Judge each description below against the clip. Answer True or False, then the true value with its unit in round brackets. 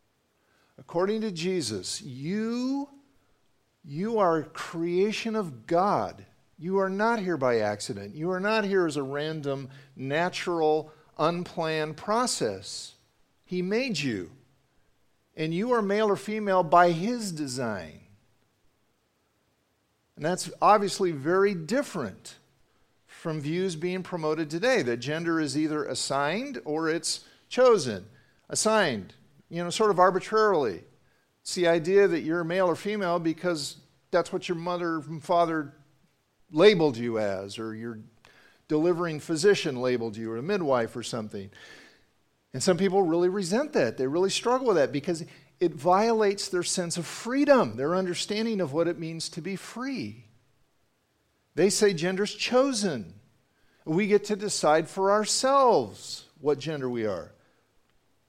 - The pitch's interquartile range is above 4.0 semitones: True (5.1 semitones)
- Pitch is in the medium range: True (175 Hz)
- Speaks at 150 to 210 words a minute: False (135 wpm)